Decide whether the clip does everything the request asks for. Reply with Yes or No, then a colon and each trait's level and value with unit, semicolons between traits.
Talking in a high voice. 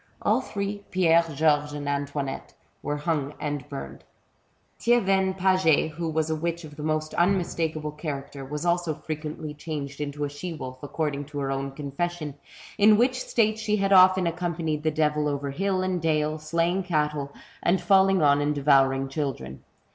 No: medium, 155 Hz